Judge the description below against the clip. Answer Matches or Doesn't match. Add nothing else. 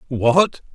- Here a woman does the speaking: Doesn't match